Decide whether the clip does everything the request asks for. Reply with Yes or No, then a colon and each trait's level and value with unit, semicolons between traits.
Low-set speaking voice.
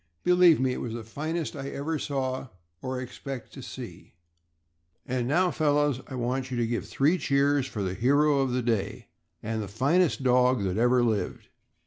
Yes: low, 130 Hz